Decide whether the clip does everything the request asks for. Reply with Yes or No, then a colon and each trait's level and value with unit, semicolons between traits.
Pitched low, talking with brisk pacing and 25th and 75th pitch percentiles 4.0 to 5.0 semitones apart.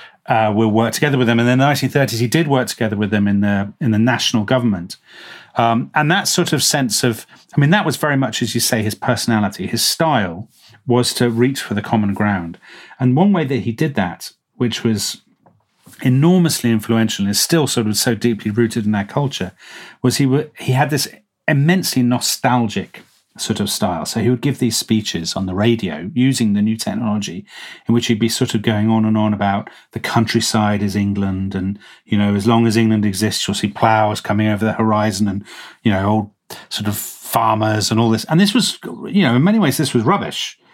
No: low, 115 Hz; fast, 215 wpm; average, 3.3 semitones